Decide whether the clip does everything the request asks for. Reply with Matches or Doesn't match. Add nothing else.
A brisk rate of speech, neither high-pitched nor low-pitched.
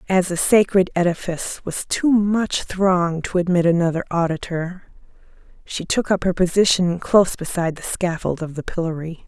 Doesn't match